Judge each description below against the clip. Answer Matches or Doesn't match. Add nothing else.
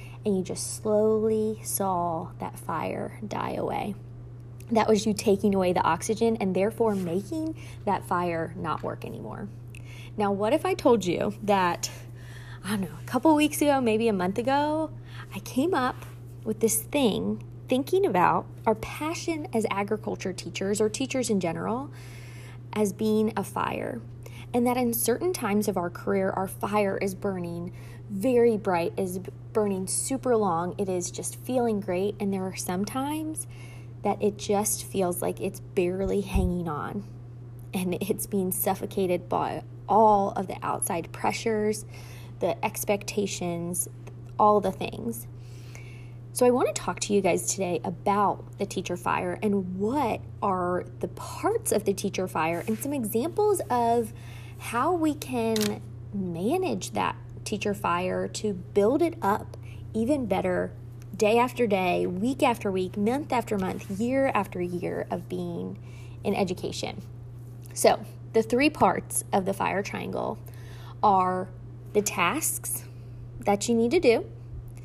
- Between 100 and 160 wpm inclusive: Matches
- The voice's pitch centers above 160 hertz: Matches